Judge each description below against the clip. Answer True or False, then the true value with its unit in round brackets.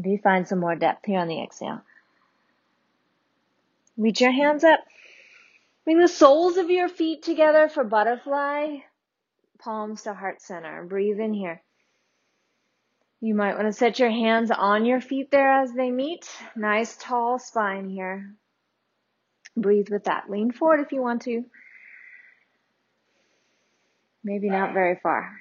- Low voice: False (230 Hz)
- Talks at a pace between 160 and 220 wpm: False (145 wpm)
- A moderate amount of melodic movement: False (5.9 semitones)